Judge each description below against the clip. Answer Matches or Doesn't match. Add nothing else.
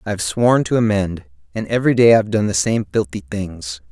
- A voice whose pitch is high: Doesn't match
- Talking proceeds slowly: Doesn't match